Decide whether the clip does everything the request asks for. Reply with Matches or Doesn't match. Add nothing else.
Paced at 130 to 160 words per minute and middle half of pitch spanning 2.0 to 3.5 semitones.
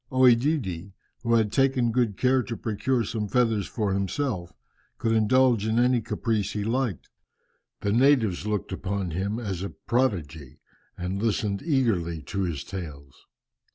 Doesn't match